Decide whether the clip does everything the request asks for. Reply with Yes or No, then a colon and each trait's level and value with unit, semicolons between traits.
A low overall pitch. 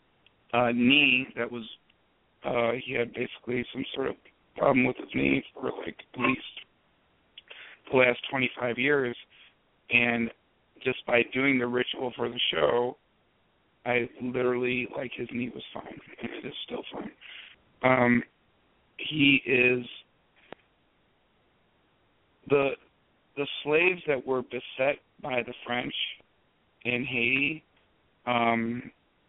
Yes: low, 125 Hz